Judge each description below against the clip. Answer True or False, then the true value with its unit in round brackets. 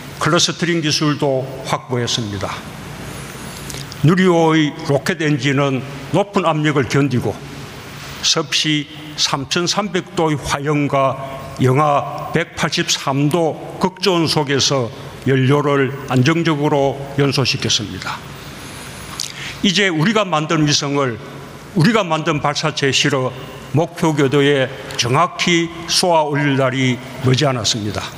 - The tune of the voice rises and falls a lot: False (3.2 semitones)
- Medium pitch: True (145 Hz)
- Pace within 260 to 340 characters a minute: False (220 characters per minute)